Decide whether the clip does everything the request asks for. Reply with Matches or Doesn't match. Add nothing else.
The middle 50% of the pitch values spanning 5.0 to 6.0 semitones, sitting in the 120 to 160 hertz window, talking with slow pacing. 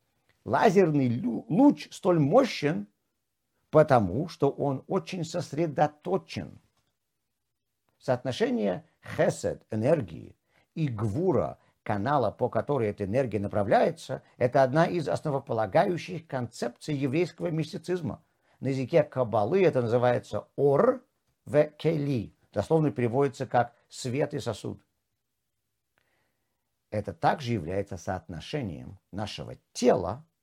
Matches